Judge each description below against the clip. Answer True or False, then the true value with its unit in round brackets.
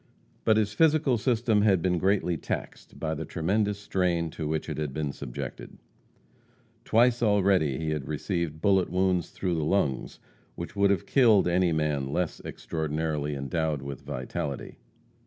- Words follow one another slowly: False (155 wpm)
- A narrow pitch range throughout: False (4.8 semitones)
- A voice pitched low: True (85 Hz)